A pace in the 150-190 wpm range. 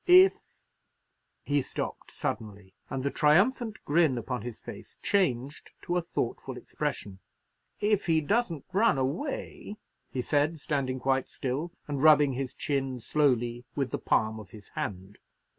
No: average, 140 wpm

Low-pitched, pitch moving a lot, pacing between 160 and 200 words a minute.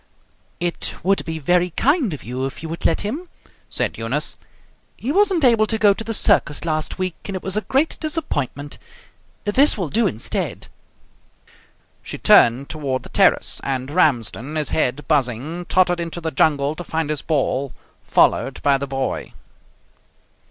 No: medium, 160 Hz; wide, 6.6 semitones; average, 165 wpm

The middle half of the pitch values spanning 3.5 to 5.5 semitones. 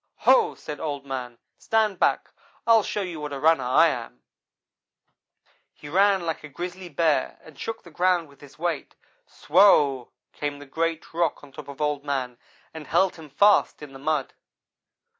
Yes: average, 3.9 semitones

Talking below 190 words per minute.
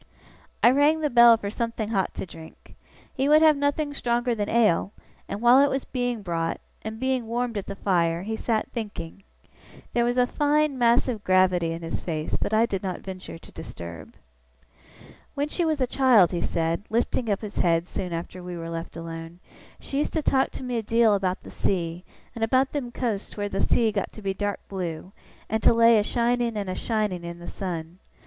No: fast, 205 wpm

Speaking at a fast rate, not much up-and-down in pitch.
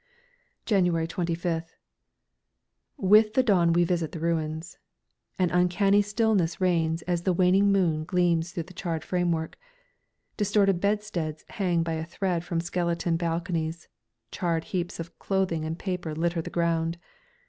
No: slow, 135 wpm; narrow, 2.2 semitones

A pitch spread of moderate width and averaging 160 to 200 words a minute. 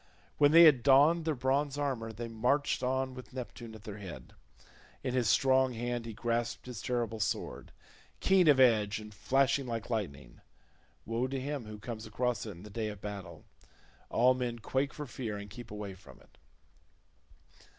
Yes: average, 3.6 semitones; average, 180 wpm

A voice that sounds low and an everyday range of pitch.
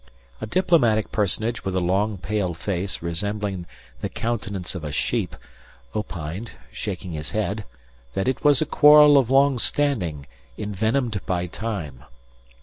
Yes: low, 105 Hz; average, 4.8 semitones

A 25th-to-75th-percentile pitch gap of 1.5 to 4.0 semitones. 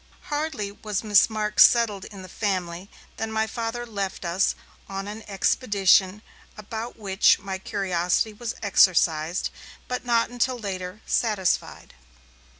Yes: average, 2.9 semitones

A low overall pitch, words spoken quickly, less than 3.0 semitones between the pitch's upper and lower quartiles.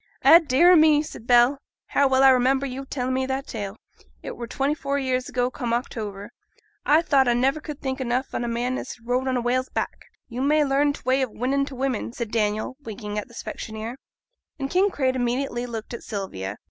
No: very high, 255 Hz; fast, 220 wpm; narrow, 2.5 semitones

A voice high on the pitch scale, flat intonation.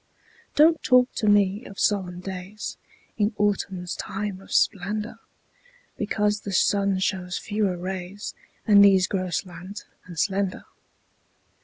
Yes: high, 195 Hz; narrow, 1.9 semitones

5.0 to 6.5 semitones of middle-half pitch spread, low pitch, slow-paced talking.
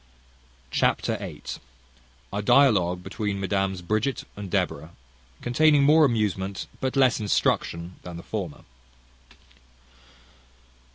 Yes: average, 5.3 semitones; low, 100 Hz; slow, 100 wpm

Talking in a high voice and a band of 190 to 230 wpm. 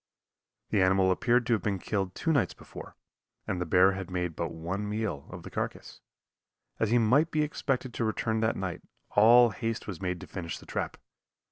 No: low, 105 Hz; average, 200 wpm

